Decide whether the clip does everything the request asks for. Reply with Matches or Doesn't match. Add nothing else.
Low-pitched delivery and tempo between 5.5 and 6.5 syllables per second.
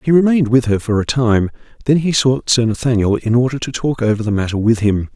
Matches